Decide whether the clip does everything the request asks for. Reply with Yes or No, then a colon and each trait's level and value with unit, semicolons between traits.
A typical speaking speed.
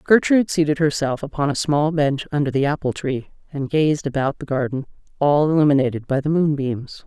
Yes: average, 180 wpm